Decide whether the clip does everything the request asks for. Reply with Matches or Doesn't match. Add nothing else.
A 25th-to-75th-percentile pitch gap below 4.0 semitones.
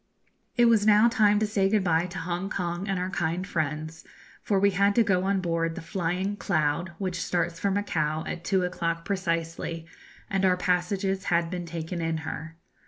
Matches